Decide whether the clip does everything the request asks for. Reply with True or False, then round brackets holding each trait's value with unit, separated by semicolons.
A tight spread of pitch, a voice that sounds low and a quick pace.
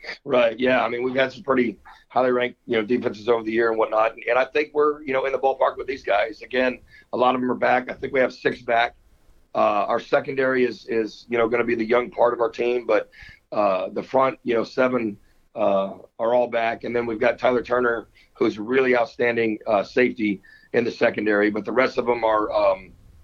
True (2.3 semitones; 120 Hz; 240 wpm)